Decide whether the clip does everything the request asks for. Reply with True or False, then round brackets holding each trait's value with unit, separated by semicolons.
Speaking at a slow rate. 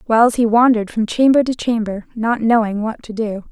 False (205 wpm)